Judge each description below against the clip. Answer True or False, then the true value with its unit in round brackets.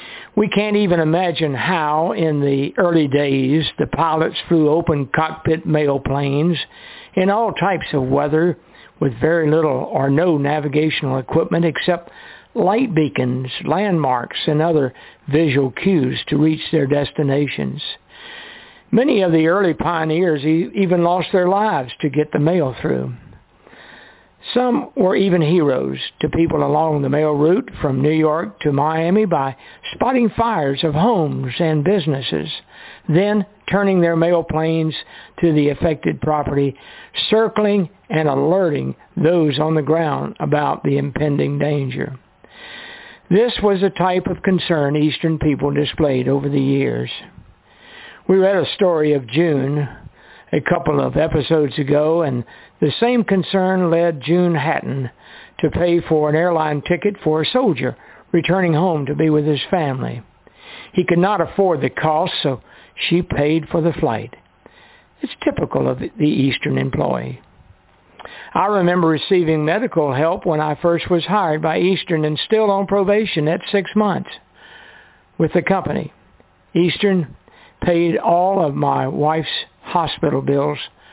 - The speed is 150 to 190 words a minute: False (140 wpm)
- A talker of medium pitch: True (160 Hz)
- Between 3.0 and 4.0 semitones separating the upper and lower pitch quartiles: True (3.6 semitones)